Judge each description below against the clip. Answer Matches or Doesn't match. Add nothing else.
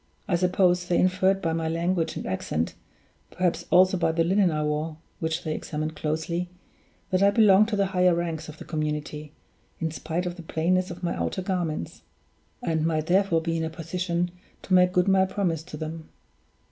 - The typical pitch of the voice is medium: Matches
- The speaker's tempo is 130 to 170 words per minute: Doesn't match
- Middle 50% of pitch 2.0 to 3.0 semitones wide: Matches